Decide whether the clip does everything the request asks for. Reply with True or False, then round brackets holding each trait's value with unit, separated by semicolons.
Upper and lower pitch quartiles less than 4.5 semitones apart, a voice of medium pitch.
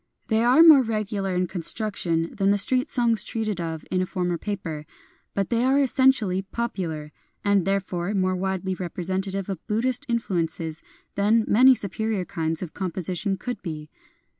False (3.8 semitones; 195 Hz)